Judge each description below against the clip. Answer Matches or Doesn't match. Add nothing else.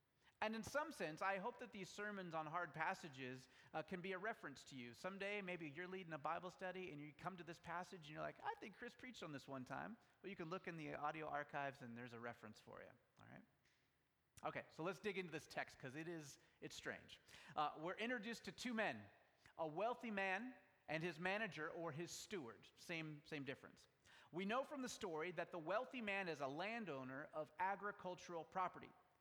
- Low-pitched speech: Doesn't match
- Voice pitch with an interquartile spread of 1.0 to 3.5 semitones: Doesn't match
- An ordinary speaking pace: Doesn't match